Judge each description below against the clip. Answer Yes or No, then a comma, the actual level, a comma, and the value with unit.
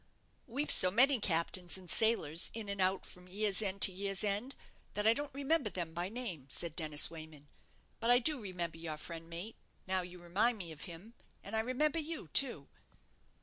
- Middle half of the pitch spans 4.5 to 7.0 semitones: Yes, average, 5.2 semitones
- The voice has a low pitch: No, high, 195 Hz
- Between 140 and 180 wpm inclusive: No, average, 190 wpm